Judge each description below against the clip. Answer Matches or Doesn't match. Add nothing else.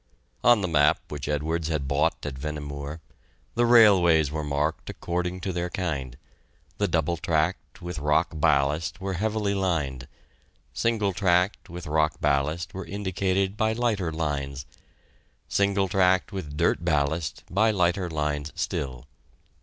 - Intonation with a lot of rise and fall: Doesn't match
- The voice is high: Doesn't match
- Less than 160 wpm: Matches